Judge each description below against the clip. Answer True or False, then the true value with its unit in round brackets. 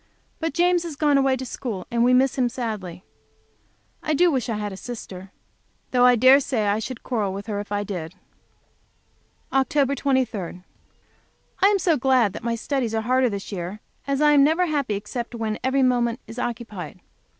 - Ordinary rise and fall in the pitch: True (4.6 semitones)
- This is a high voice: True (245 Hz)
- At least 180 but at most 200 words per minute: True (185 wpm)